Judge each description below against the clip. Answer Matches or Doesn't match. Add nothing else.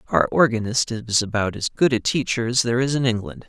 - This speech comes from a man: Matches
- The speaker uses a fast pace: Matches